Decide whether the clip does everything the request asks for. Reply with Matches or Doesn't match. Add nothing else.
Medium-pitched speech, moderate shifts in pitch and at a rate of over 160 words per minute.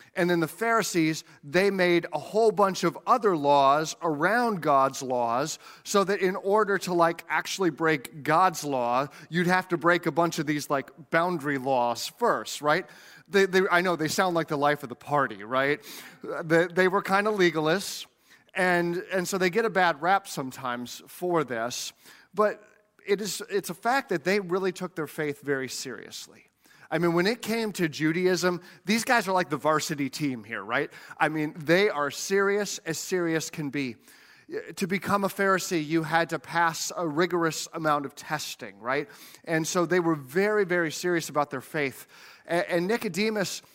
Matches